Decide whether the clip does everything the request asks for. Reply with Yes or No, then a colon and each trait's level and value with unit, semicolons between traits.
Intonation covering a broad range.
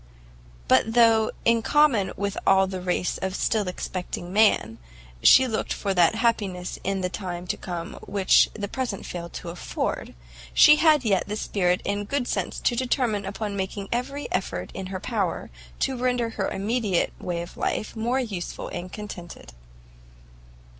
No: average, 4.1 semitones